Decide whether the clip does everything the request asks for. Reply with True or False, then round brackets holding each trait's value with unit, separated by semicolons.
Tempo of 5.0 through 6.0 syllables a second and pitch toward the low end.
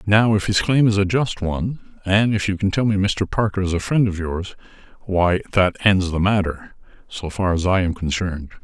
True (5.2 syllables/s; 95 Hz)